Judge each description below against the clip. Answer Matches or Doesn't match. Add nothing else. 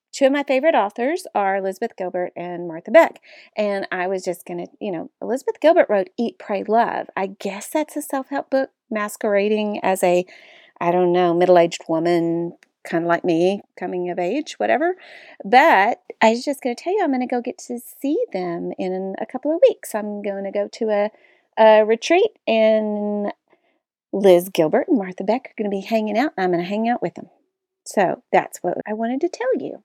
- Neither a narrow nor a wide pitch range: Doesn't match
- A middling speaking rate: Doesn't match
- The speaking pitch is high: Matches